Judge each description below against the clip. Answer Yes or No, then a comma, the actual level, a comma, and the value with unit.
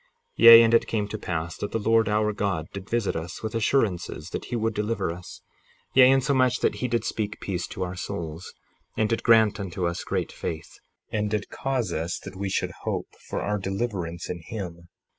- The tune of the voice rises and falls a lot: No, average, 4.2 semitones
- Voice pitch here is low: Yes, low, 105 Hz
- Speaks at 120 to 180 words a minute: No, fast, 205 wpm